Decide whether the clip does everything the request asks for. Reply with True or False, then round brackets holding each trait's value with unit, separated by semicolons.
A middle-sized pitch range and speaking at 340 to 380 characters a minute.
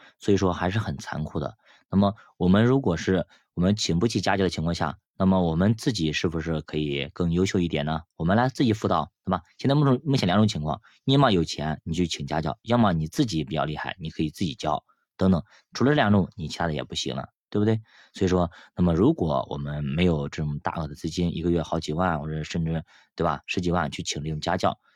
True (3.7 semitones; 345 characters per minute)